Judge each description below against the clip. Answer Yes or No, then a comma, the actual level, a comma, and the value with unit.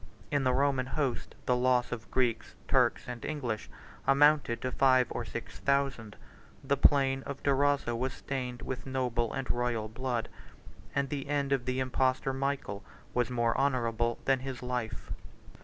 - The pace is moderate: Yes, average, 160 wpm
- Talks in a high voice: No, low, 130 Hz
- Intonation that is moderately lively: No, narrow, 2.0 semitones